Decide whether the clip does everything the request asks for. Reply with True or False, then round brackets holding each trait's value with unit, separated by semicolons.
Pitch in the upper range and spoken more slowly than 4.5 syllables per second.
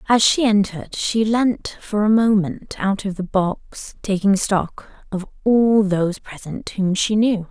True (200 Hz; 4.0 syllables/s)